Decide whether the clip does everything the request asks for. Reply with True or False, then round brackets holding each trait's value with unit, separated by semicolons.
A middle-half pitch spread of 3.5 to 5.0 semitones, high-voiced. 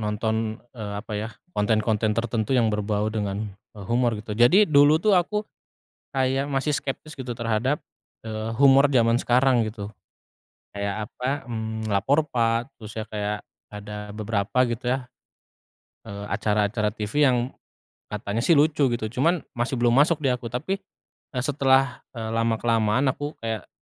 False (3.8 semitones; 115 Hz)